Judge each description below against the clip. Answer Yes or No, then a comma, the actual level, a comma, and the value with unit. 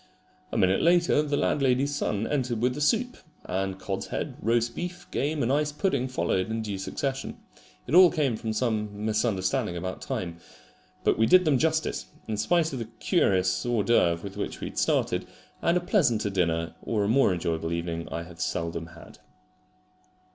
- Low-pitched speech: Yes, low, 115 Hz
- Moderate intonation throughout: No, wide, 7.5 semitones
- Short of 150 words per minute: No, average, 180 wpm